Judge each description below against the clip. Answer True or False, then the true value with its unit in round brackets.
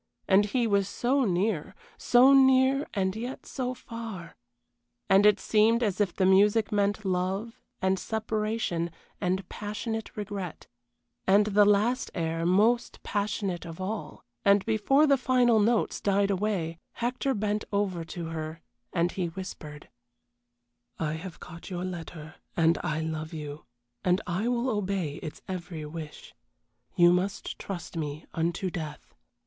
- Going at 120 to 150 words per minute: True (145 wpm)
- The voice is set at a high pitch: True (195 Hz)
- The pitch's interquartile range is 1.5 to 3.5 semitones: False (4.2 semitones)